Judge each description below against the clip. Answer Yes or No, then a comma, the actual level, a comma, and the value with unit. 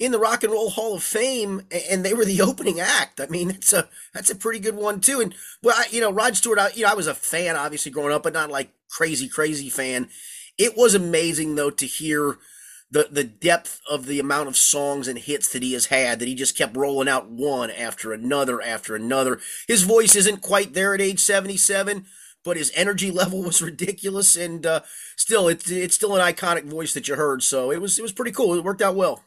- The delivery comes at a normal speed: No, fast, 235 wpm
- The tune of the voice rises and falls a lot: Yes, wide, 6.0 semitones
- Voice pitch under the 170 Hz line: No, medium, 175 Hz